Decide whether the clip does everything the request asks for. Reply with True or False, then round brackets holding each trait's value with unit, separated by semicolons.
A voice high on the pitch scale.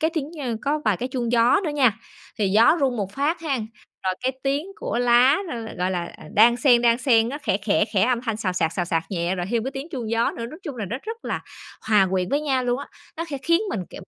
True (240 Hz)